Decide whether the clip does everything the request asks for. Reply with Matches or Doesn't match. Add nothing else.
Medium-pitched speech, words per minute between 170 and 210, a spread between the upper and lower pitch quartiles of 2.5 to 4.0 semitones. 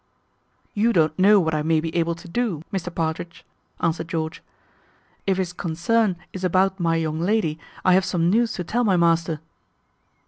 Matches